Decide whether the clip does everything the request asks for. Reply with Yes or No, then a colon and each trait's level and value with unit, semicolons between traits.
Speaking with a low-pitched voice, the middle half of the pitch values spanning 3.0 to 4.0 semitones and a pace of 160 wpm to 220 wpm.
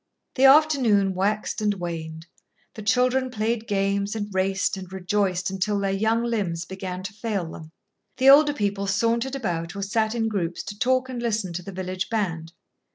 No: high, 200 Hz; average, 3.5 semitones; average, 175 wpm